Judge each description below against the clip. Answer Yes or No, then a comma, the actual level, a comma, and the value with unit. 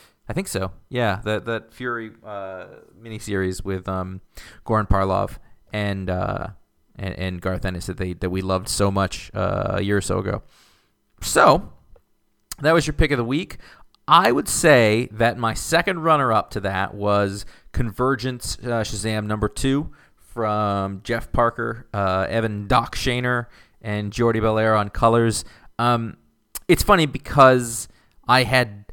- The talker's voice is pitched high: No, low, 105 Hz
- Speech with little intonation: No, average, 3.6 semitones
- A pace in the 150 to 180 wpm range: Yes, average, 155 wpm